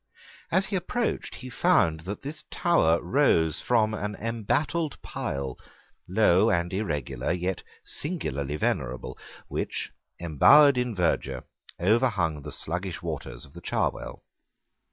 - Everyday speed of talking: No, slow, 120 wpm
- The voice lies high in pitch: No, low, 100 Hz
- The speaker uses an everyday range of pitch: No, wide, 8.2 semitones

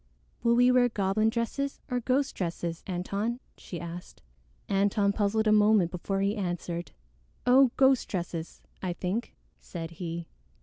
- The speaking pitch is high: Yes, high, 200 Hz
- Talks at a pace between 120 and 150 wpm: Yes, average, 140 wpm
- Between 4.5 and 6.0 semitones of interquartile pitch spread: Yes, average, 4.9 semitones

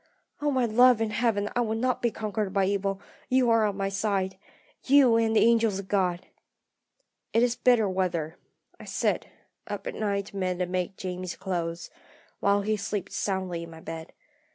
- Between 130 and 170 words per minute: No, average, 185 wpm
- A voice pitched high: Yes, high, 200 Hz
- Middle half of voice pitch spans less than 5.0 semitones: Yes, average, 3.4 semitones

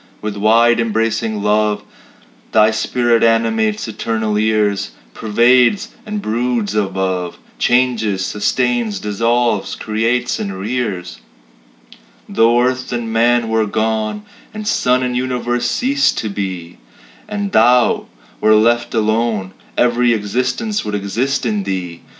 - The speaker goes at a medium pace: No, slow, 115 wpm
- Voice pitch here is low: Yes, low, 115 Hz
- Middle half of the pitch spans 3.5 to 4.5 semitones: No, average, 2.7 semitones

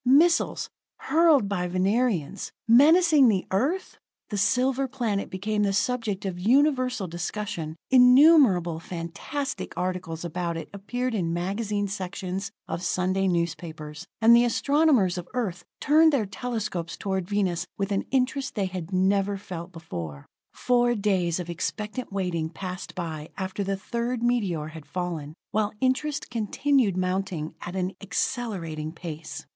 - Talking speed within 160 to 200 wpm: No, slow, 135 wpm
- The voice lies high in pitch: Yes, high, 195 Hz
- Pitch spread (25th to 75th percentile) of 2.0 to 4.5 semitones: No, wide, 5.6 semitones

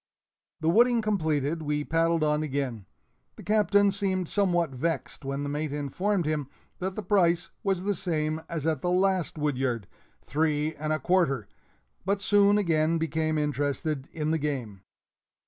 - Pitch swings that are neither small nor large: Yes, average, 4.1 semitones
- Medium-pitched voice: Yes, medium, 160 Hz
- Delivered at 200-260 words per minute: No, average, 155 wpm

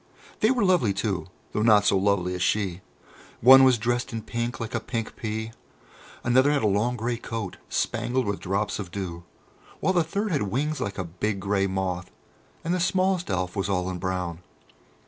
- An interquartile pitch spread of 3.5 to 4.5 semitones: No, average, 4.9 semitones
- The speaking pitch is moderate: No, low, 105 Hz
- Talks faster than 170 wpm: Yes, average, 190 wpm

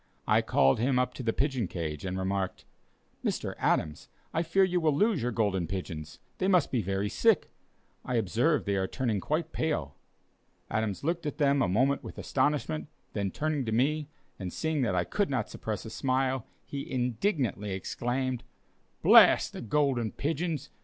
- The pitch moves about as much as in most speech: No, wide, 7.0 semitones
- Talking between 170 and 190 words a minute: Yes, average, 175 wpm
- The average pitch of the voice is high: No, low, 125 Hz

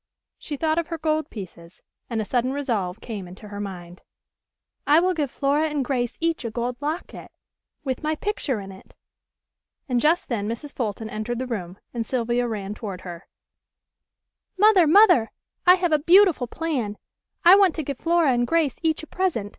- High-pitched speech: Yes, very high, 255 Hz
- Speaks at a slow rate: No, average, 180 wpm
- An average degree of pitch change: No, wide, 6.6 semitones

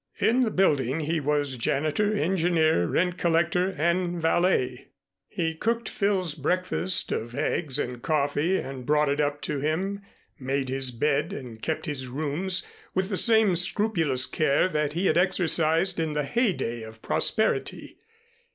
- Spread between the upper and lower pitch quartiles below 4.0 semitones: No, average, 4.7 semitones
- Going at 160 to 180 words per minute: No, average, 150 wpm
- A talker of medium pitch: Yes, medium, 160 Hz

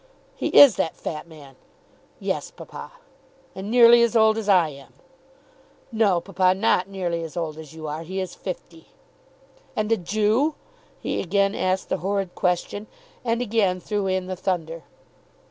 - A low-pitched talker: No, high, 190 Hz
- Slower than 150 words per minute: No, average, 160 wpm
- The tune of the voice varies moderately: Yes, average, 4.1 semitones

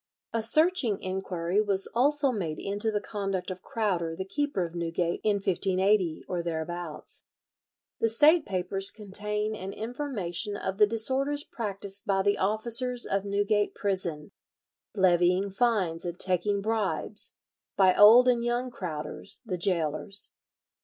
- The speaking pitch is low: No, high, 200 Hz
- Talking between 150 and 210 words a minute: No, slow, 135 wpm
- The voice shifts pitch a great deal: No, average, 3.5 semitones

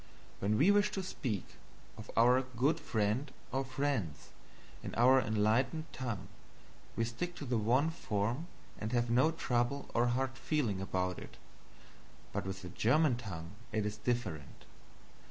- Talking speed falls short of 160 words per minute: Yes, average, 150 wpm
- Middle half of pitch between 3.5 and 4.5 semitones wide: Yes, average, 4.2 semitones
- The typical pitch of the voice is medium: No, low, 120 Hz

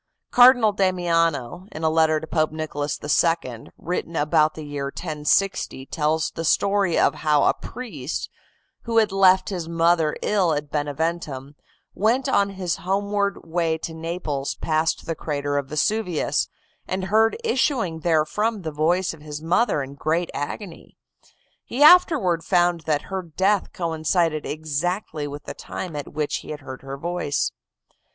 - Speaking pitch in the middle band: Yes, medium, 165 Hz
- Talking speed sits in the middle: Yes, average, 150 wpm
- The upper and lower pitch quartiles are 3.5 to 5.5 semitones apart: Yes, average, 3.9 semitones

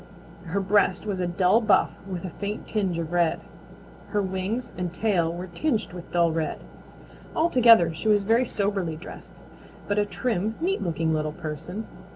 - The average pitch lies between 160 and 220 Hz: Yes, high, 190 Hz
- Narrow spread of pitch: No, average, 3.8 semitones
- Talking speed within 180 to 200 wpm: No, average, 170 wpm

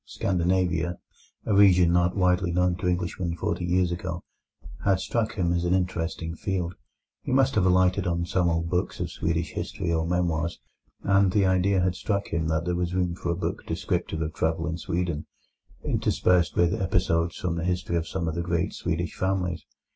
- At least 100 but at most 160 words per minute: No, average, 185 wpm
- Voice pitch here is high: No, very low, 90 Hz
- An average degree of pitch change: No, narrow, 1.6 semitones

